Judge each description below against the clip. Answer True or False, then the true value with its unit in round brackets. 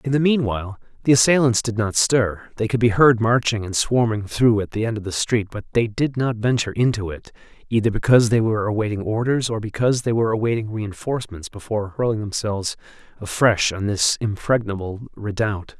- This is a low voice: True (110 Hz)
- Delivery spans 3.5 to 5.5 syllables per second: False (5.8 syllables/s)